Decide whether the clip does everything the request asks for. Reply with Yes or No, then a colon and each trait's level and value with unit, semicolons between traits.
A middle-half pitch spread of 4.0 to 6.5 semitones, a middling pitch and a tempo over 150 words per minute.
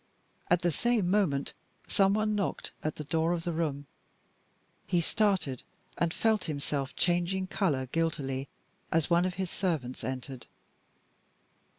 No: average, 4.9 semitones; medium, 170 Hz; slow, 135 wpm